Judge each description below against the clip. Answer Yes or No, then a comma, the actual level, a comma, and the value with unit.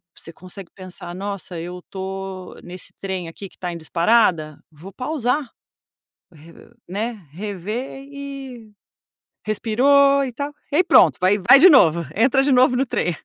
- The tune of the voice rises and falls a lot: Yes, wide, 6.4 semitones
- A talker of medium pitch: No, high, 205 Hz